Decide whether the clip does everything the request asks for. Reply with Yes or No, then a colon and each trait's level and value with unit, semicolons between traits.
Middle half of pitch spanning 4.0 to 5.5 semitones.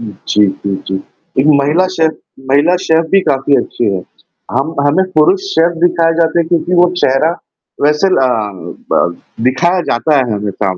Yes: average, 4.8 semitones